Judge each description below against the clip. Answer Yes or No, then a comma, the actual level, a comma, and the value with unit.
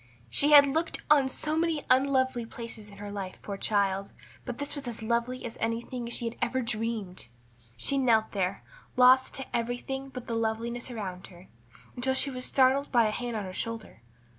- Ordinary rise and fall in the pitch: Yes, average, 3.2 semitones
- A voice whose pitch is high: Yes, high, 235 Hz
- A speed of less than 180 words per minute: No, average, 190 wpm